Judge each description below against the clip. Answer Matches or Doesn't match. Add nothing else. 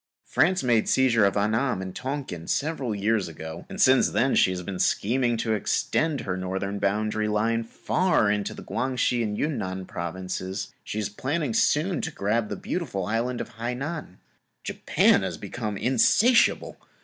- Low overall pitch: Matches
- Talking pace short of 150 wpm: Doesn't match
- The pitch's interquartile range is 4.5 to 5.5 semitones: Matches